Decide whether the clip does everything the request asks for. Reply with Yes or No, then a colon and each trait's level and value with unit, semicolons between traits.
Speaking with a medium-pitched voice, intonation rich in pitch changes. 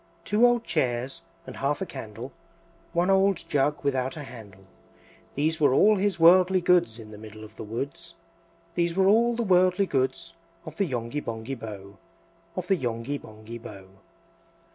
Yes: medium, 145 Hz; wide, 8.0 semitones